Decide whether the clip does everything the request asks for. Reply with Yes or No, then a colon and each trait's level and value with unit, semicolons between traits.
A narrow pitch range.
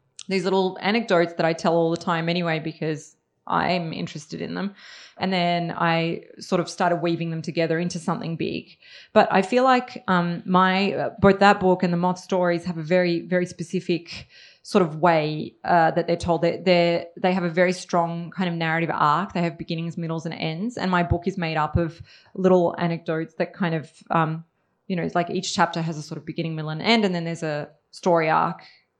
Yes: narrow, 1.9 semitones